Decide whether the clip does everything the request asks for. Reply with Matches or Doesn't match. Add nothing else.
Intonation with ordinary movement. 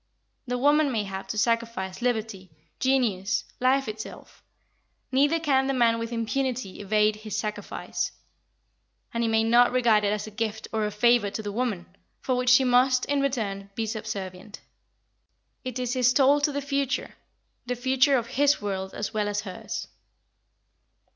Matches